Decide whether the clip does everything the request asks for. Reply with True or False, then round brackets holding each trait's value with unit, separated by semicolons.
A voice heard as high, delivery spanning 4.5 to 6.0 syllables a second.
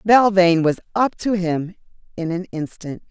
False (180 Hz; 4.6 syllables/s)